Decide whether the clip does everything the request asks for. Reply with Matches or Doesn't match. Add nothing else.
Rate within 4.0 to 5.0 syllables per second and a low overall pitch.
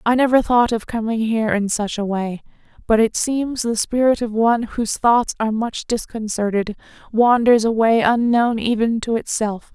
Doesn't match